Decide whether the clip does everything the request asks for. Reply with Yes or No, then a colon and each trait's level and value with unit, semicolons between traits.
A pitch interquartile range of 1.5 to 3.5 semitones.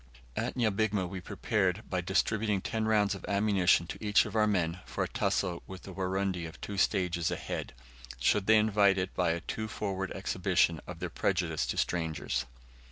Yes: average, 2.7 semitones